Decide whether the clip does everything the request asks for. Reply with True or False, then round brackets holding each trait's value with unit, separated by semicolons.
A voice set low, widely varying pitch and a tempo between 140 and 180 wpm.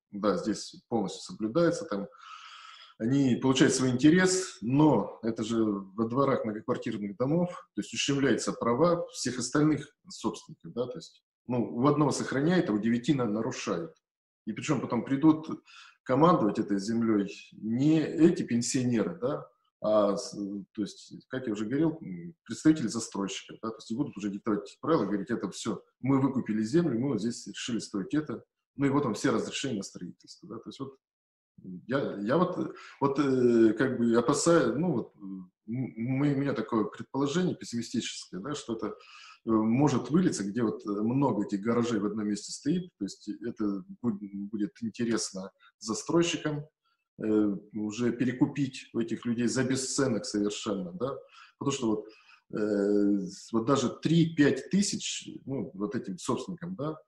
True (120 Hz; 5.8 semitones; 150 wpm)